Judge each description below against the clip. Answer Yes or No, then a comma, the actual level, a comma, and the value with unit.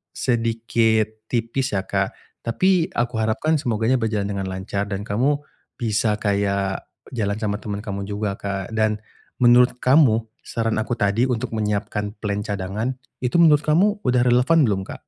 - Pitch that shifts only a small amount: No, average, 3.4 semitones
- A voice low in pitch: Yes, low, 110 Hz